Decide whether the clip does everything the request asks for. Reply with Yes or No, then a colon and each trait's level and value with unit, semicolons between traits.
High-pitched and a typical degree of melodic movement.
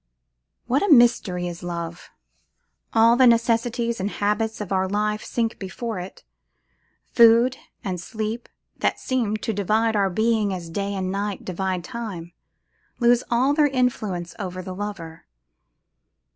Yes: high, 210 Hz; average, 4.0 semitones